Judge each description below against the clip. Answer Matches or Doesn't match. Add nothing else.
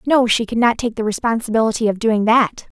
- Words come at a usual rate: Doesn't match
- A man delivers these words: Doesn't match